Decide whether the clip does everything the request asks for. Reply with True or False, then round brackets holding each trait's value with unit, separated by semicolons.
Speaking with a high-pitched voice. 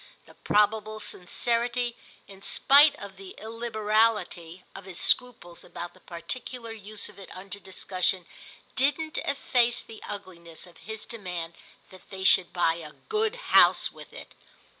True (210 Hz)